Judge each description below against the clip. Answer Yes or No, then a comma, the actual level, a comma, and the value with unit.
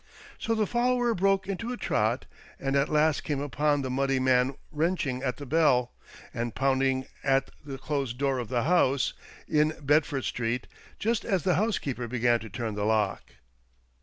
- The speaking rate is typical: Yes, average, 170 wpm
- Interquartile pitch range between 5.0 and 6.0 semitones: No, average, 4.1 semitones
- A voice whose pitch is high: No, low, 135 Hz